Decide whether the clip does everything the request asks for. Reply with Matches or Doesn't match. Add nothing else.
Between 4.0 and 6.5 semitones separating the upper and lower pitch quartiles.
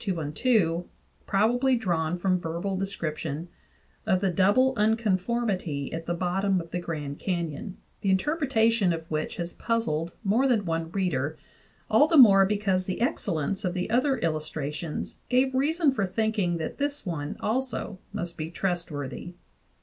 Matches